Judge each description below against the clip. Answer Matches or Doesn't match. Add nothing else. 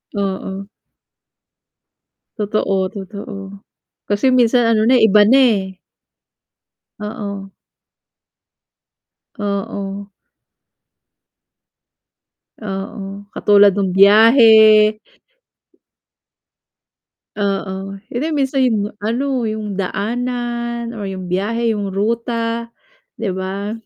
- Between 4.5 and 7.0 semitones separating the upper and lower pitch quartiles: Doesn't match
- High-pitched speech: Matches